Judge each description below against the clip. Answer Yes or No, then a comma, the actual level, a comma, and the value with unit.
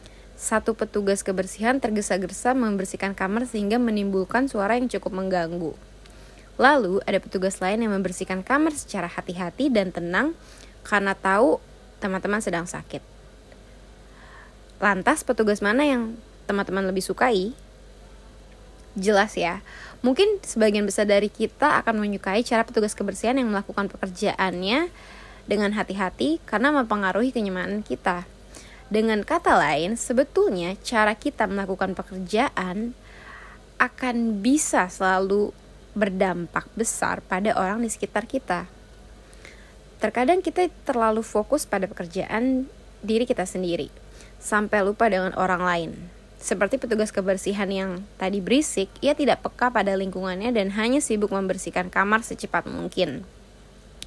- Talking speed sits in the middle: Yes, average, 120 wpm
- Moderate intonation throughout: Yes, average, 3.6 semitones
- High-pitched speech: Yes, high, 205 Hz